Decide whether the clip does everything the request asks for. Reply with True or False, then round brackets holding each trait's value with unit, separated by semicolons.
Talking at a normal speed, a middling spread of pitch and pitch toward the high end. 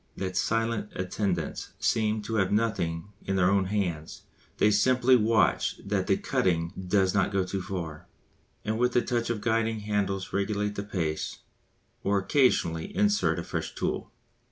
False (160 wpm; 3.3 semitones; 100 Hz)